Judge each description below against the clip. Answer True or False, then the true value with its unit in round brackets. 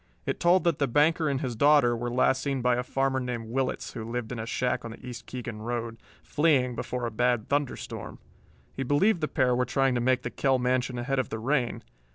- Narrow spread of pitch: True (2.1 semitones)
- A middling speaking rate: False (230 wpm)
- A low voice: True (125 Hz)